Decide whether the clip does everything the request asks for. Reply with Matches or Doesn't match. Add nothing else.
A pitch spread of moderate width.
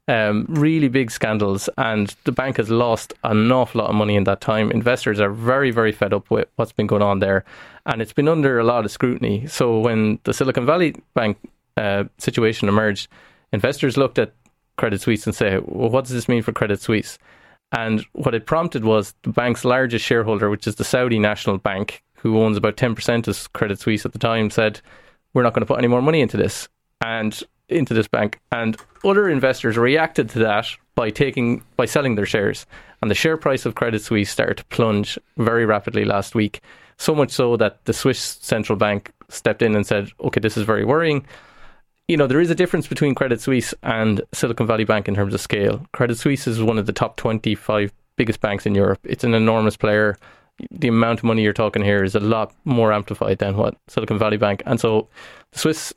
Matches